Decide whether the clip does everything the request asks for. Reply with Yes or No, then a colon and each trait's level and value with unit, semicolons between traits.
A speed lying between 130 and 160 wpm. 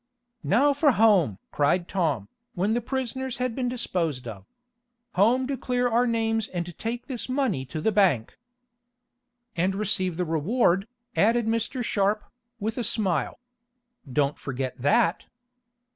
Yes: average, 140 wpm